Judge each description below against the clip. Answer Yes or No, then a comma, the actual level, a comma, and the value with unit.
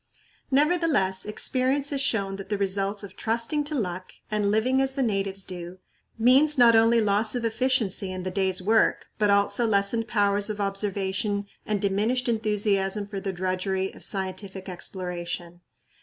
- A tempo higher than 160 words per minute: No, average, 155 wpm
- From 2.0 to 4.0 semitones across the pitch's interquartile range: Yes, average, 3.3 semitones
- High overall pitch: Yes, high, 205 Hz